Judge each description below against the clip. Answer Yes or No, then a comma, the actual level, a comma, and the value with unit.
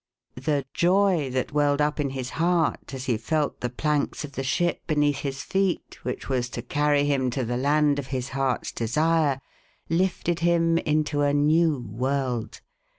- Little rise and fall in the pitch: No, average, 3.2 semitones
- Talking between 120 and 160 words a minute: No, average, 170 wpm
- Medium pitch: Yes, medium, 145 Hz